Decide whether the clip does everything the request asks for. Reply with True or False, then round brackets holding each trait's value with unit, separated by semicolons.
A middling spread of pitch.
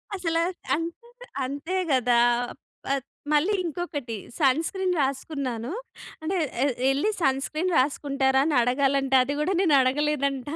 True (3.7 semitones)